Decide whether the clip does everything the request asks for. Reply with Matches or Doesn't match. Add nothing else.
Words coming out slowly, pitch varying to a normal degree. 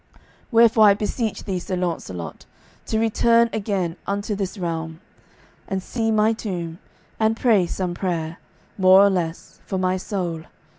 Doesn't match